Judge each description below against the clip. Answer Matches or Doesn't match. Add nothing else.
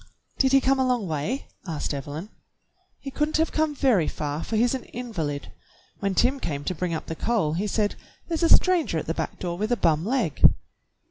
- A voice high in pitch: Matches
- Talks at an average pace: Doesn't match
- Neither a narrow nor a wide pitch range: Doesn't match